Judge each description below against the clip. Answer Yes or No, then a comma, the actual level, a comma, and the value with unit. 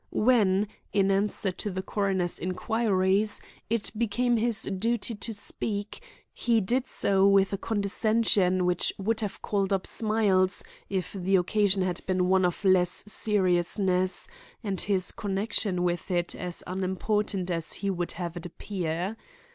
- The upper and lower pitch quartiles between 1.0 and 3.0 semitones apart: Yes, narrow, 2.4 semitones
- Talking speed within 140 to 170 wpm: Yes, average, 145 wpm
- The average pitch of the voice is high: Yes, high, 195 Hz